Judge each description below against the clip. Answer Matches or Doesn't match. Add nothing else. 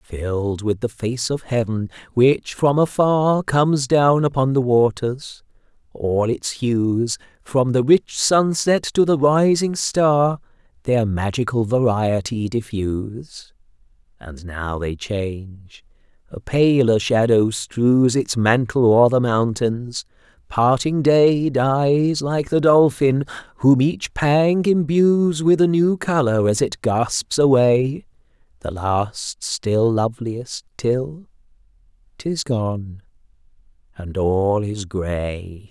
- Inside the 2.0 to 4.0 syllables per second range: Matches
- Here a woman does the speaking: Doesn't match